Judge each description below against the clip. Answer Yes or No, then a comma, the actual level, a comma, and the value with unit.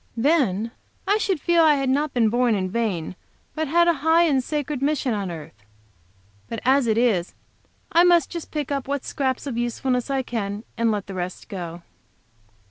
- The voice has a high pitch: Yes, very high, 255 Hz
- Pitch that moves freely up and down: Yes, wide, 5.9 semitones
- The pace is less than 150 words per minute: No, average, 195 wpm